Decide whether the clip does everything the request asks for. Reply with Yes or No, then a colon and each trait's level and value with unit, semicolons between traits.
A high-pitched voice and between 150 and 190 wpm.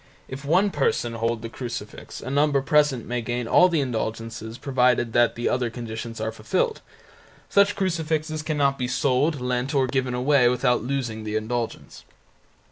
No: low, 125 Hz; average, 160 wpm